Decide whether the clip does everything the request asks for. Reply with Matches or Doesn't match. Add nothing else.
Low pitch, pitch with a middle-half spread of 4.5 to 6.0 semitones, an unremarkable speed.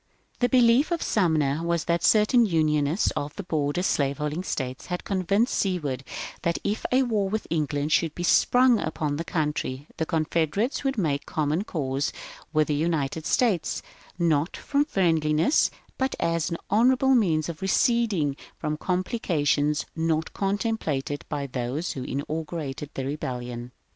Doesn't match